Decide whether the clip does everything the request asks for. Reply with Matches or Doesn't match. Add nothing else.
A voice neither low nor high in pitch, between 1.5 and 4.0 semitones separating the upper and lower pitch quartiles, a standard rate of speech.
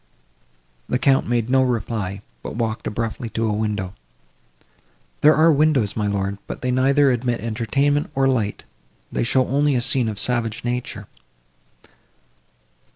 Doesn't match